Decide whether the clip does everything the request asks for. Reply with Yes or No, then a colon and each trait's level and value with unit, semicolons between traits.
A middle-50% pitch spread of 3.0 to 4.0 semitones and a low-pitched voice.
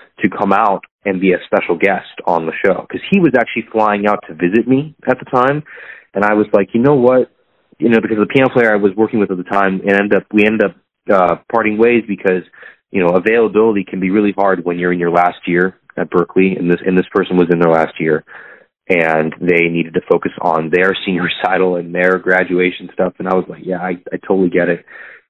Yes: average, 3.6 semitones; very low, 95 Hz